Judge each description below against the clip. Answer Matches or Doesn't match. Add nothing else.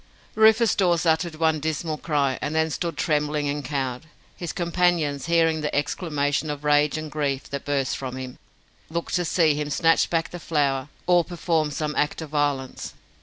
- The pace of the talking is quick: Doesn't match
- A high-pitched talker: Doesn't match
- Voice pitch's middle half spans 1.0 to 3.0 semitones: Matches